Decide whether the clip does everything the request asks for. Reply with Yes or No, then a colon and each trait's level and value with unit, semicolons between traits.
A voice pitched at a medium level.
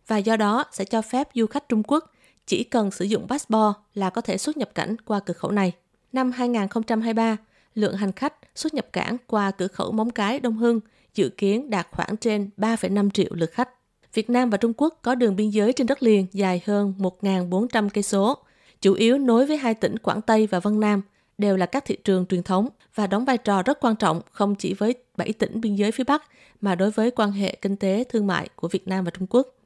No: high, 215 Hz